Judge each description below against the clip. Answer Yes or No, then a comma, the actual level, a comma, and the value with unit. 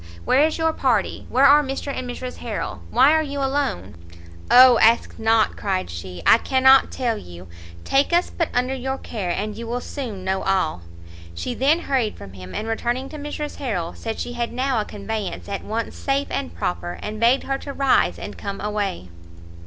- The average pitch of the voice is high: Yes, high, 235 Hz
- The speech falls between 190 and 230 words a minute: Yes, average, 195 wpm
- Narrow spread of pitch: No, wide, 5.4 semitones